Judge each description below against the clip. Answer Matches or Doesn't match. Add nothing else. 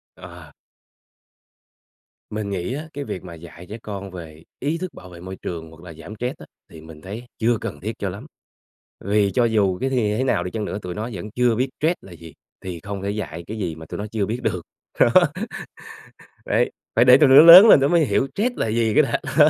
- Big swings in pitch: Matches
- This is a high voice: Doesn't match